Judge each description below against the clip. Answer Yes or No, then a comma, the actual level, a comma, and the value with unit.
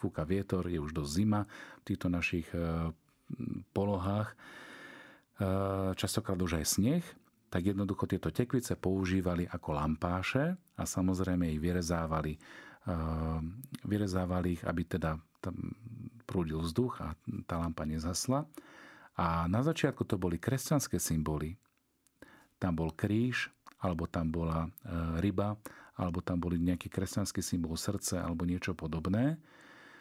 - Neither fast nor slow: Yes, average, 120 wpm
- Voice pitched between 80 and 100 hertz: Yes, very low, 90 Hz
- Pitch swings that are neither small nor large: Yes, average, 4.0 semitones